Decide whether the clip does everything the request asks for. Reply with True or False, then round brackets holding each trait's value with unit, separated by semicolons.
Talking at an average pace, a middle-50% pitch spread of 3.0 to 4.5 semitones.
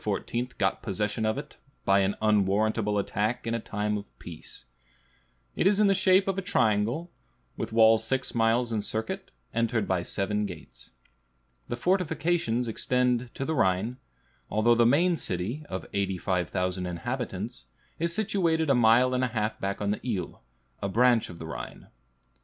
True (155 wpm; 4.2 semitones)